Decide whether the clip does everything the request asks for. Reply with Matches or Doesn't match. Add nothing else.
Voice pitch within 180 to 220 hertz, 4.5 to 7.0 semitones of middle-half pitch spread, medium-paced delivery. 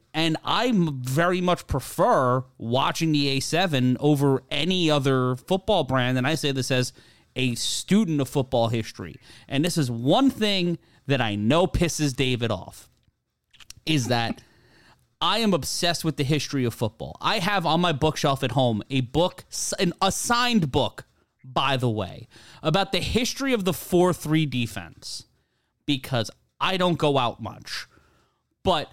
Doesn't match